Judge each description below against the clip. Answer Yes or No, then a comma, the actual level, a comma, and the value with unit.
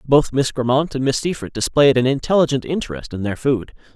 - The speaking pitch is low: Yes, low, 130 Hz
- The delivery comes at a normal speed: Yes, average, 195 wpm